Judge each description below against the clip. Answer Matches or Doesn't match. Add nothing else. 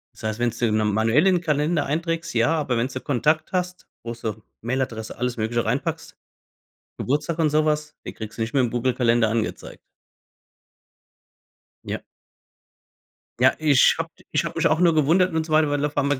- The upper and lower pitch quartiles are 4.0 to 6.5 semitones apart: Matches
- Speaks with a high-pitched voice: Doesn't match